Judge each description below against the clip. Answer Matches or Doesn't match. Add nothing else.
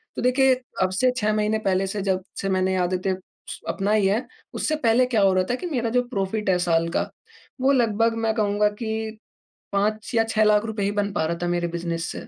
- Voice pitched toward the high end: Matches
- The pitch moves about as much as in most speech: Matches